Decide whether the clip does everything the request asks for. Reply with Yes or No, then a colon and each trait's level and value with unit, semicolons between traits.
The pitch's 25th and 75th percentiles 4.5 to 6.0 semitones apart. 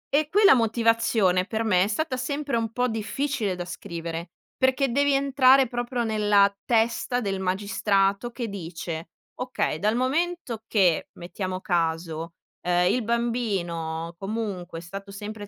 Yes: average, 5.3 semitones